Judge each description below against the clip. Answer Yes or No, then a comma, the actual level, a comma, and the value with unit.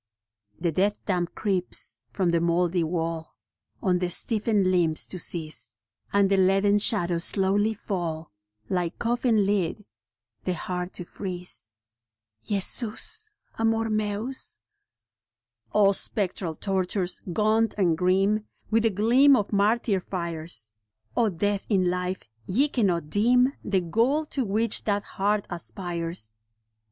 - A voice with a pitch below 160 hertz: No, high, 195 Hz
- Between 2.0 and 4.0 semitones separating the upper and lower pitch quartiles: Yes, average, 3.4 semitones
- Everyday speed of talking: No, slow, 125 wpm